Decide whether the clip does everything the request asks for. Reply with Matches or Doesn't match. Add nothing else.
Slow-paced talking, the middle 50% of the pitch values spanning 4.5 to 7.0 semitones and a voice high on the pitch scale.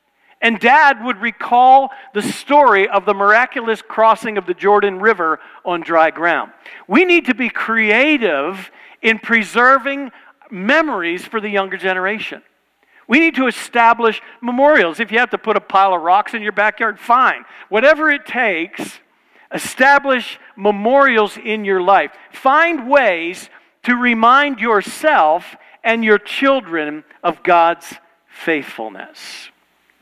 Matches